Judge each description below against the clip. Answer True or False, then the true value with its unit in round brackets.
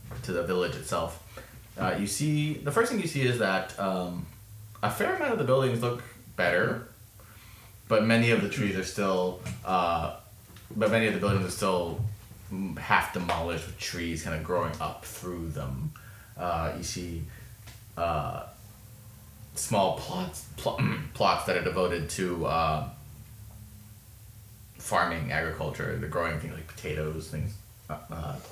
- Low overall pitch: True (105 Hz)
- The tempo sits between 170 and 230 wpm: False (145 wpm)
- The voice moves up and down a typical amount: True (3.8 semitones)